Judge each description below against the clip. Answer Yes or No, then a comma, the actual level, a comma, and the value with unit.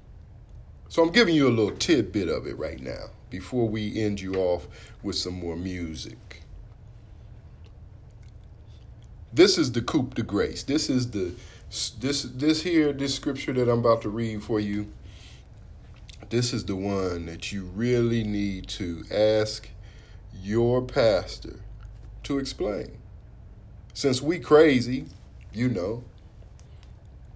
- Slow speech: Yes, slow, 130 wpm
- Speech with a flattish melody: No, average, 3.5 semitones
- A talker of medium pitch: No, low, 110 Hz